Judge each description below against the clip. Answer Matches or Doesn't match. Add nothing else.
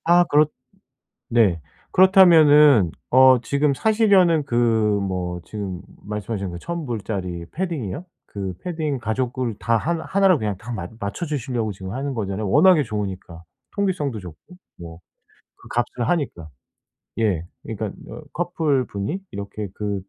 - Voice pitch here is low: Matches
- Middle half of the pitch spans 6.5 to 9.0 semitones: Matches